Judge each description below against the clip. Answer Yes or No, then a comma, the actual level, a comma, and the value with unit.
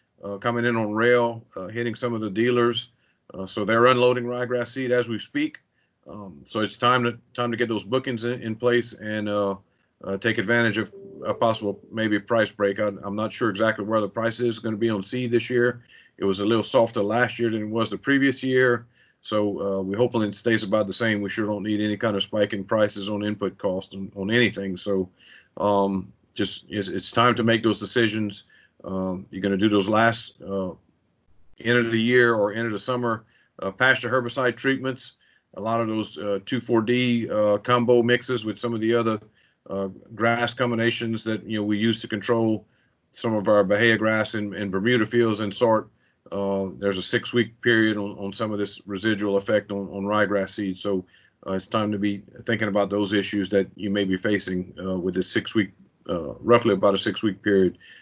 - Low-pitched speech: Yes, low, 110 Hz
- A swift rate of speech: Yes, fast, 210 wpm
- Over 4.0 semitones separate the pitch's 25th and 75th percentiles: No, average, 2.9 semitones